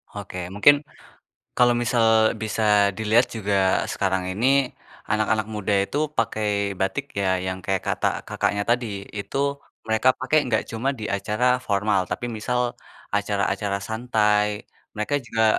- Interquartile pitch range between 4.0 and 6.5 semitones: No, average, 3.1 semitones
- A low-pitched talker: Yes, low, 110 Hz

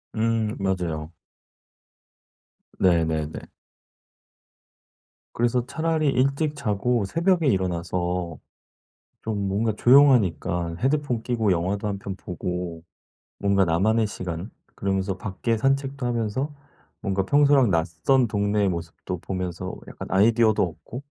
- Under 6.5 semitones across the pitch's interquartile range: Yes, wide, 5.4 semitones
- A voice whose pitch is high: No, low, 100 Hz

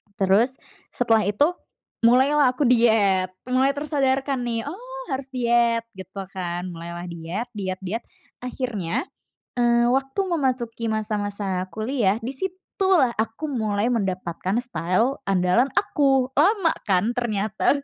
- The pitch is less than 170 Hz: No, high, 235 Hz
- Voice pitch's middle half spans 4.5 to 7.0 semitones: Yes, average, 5.1 semitones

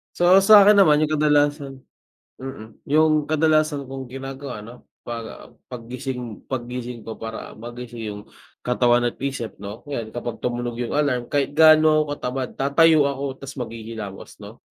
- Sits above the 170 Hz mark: No, low, 130 Hz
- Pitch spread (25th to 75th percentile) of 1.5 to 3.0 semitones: No, average, 3.7 semitones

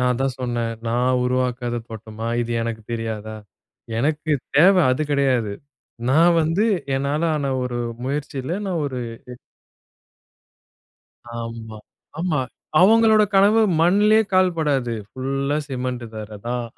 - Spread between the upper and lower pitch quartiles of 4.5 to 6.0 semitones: Yes, average, 5.0 semitones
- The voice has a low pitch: Yes, low, 130 Hz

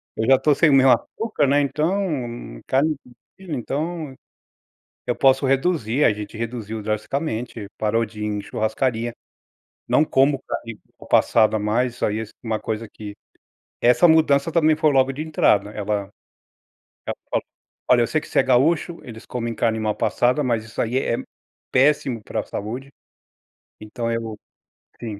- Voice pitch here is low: Yes, low, 120 Hz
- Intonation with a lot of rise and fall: No, average, 4.4 semitones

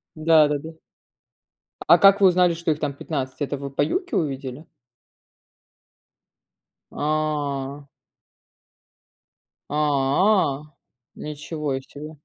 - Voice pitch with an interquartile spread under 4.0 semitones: Yes, narrow, 2.5 semitones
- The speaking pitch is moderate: Yes, medium, 150 Hz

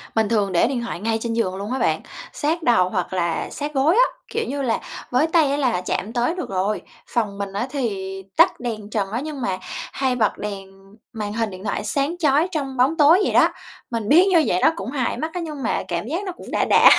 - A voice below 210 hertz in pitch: No, high, 240 Hz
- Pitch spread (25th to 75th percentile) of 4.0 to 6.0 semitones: No, wide, 6.4 semitones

